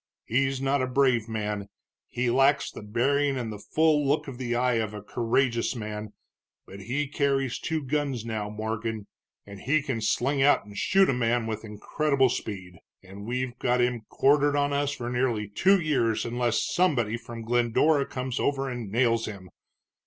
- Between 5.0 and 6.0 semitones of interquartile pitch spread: No, average, 3.8 semitones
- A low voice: Yes, low, 120 Hz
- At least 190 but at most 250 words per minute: No, average, 175 wpm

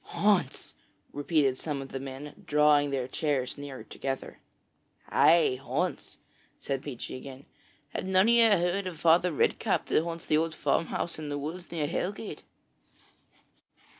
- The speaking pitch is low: No, medium, 150 Hz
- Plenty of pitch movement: No, average, 4.0 semitones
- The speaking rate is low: No, average, 145 wpm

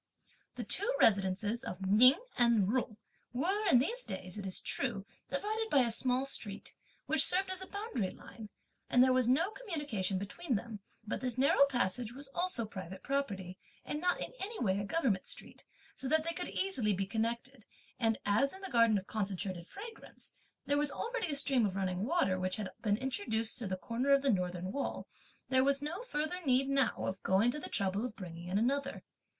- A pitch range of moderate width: No, wide, 6.3 semitones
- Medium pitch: No, high, 245 Hz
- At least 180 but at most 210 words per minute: Yes, average, 200 wpm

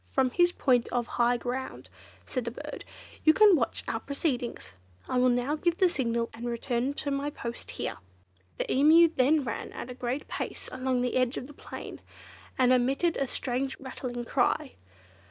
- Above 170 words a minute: Yes, average, 180 wpm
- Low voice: No, very high, 255 Hz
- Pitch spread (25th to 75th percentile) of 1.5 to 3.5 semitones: Yes, average, 2.7 semitones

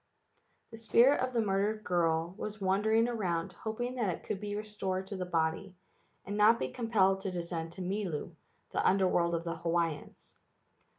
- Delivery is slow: No, average, 175 wpm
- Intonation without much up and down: No, average, 3.8 semitones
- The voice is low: No, high, 195 Hz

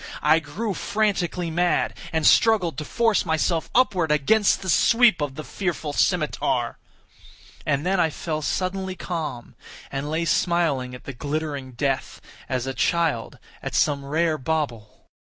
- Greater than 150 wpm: No, average, 145 wpm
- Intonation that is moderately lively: Yes, average, 4.0 semitones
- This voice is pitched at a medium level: Yes, medium, 160 Hz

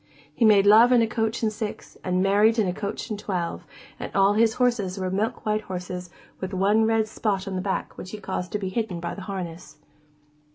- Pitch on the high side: Yes, high, 200 Hz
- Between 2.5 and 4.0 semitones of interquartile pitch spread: Yes, average, 2.8 semitones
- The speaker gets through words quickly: Yes, fast, 220 wpm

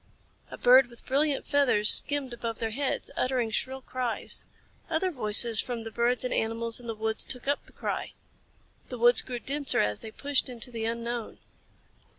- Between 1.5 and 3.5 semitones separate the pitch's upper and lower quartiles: Yes, average, 2.7 semitones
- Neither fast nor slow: Yes, average, 175 wpm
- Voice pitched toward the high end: Yes, high, 240 Hz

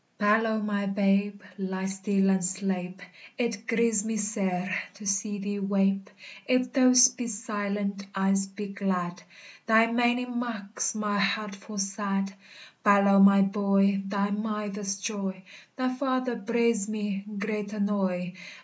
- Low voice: No, high, 205 Hz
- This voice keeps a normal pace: No, slow, 130 wpm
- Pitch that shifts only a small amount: Yes, narrow, 1.9 semitones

